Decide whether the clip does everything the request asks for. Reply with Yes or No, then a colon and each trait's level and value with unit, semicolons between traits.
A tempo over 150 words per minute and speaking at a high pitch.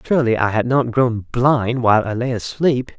No: average, 200 wpm; low, 120 Hz